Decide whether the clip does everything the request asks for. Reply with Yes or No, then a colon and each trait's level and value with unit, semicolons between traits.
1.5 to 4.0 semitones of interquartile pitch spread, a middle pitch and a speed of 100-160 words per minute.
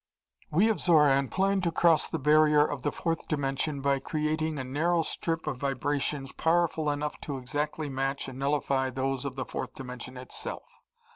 No: narrow, 2.6 semitones; medium, 145 Hz; average, 170 wpm